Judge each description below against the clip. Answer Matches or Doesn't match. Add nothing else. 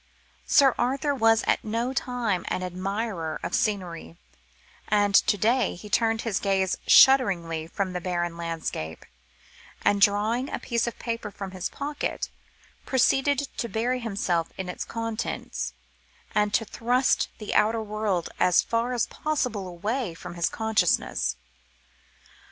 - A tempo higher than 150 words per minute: Doesn't match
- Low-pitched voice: Doesn't match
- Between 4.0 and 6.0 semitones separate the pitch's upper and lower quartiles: Matches